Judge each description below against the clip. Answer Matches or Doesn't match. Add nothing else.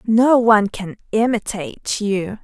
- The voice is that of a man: Doesn't match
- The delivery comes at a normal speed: Doesn't match